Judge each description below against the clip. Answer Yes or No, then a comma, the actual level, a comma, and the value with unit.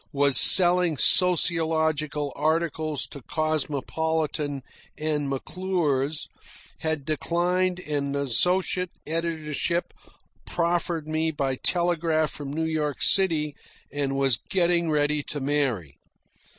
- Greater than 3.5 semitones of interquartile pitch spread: No, average, 2.9 semitones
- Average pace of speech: No, slow, 100 wpm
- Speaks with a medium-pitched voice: Yes, medium, 155 Hz